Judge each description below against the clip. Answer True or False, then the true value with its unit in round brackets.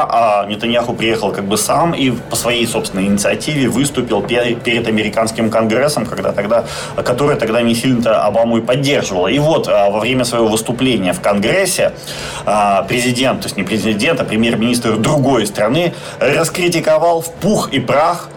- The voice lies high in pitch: False (115 Hz)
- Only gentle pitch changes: True (2.2 semitones)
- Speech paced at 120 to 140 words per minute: False (150 wpm)